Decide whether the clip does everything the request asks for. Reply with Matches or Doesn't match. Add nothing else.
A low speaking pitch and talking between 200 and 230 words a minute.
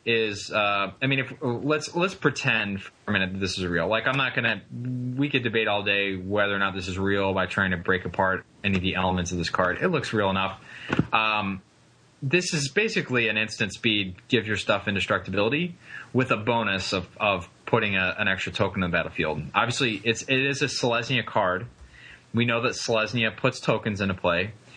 Matches